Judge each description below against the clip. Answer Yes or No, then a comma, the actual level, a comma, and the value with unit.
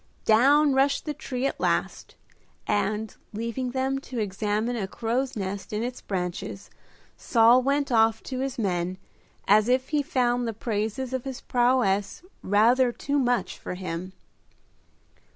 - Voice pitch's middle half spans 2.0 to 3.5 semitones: No, average, 3.9 semitones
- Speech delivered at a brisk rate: No, average, 145 wpm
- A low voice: No, high, 240 Hz